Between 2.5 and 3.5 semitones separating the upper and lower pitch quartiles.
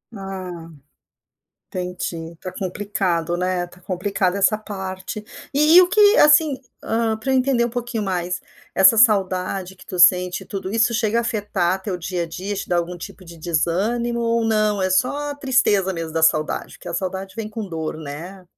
No: average, 3.9 semitones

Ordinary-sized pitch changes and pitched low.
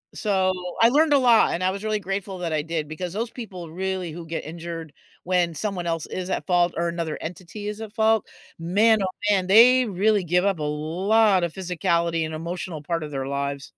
No: average, 3.8 semitones; medium, 180 Hz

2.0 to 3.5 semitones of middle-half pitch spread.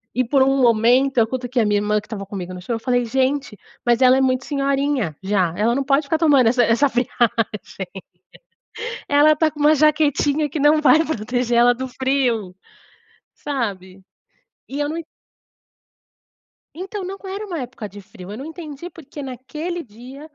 No: average, 4.4 semitones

